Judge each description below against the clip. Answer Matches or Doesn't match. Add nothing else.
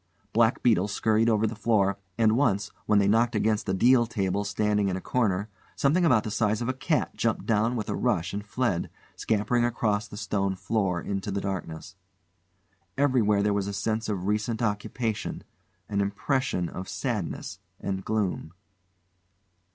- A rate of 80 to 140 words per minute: Doesn't match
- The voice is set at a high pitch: Doesn't match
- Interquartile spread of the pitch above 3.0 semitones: Doesn't match